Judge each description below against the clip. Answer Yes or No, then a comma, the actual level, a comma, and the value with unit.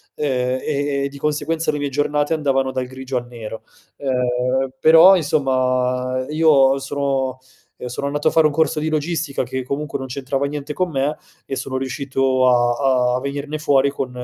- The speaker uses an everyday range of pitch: No, narrow, 2.2 semitones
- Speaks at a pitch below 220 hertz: Yes, low, 135 Hz